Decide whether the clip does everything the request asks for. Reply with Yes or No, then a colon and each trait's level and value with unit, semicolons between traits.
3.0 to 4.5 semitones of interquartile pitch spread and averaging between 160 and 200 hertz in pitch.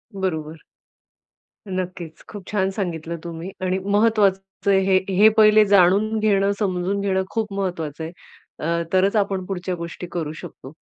No: narrow, 2.4 semitones; high, 190 Hz